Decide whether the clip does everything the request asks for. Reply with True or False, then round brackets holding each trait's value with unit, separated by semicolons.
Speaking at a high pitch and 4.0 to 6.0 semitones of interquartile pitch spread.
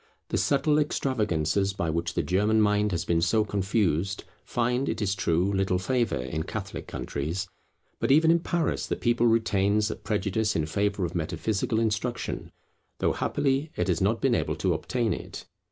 False (100 Hz; 4.7 semitones)